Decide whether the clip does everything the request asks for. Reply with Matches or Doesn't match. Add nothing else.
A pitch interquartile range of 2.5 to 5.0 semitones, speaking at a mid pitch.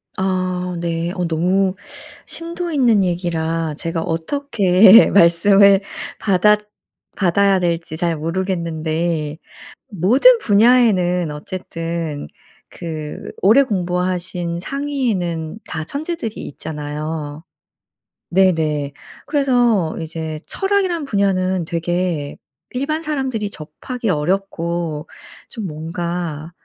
Matches